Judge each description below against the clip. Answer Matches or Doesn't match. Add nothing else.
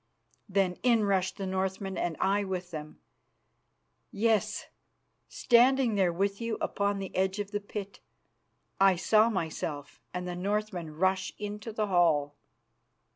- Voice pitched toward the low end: Doesn't match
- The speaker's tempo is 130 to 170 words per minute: Matches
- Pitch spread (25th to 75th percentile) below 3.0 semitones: Matches